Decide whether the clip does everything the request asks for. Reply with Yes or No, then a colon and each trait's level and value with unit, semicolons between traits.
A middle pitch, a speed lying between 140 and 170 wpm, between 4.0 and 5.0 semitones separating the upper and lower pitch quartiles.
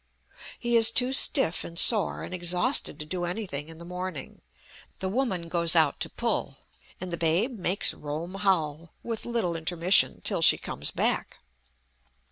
Yes: medium, 180 Hz; average, 160 wpm; average, 4.3 semitones